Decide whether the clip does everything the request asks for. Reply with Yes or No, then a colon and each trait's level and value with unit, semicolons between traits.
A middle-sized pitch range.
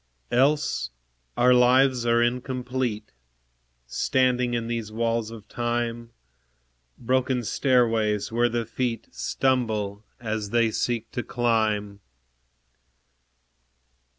No: narrow, 1.9 semitones